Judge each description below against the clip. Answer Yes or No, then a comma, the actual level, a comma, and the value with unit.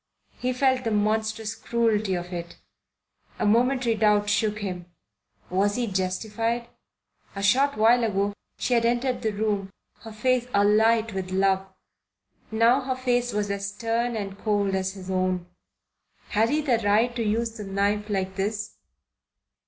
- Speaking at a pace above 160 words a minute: No, average, 155 wpm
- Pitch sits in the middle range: No, high, 215 Hz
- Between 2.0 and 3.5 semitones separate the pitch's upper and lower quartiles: Yes, average, 2.8 semitones